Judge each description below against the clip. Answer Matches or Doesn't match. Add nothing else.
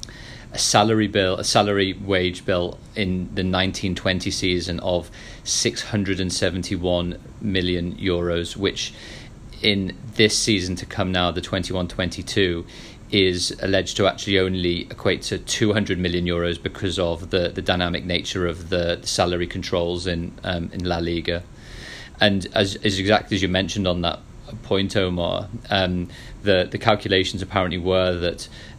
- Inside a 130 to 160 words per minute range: Matches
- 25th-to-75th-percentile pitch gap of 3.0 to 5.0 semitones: Doesn't match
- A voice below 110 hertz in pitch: Matches